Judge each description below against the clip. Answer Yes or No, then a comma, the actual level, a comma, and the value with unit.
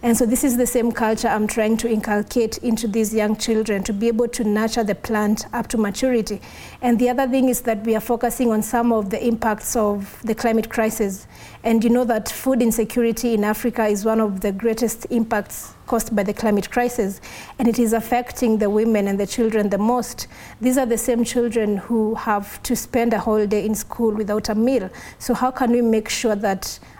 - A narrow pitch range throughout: Yes, narrow, 1.9 semitones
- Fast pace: Yes, fast, 215 wpm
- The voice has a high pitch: Yes, high, 225 Hz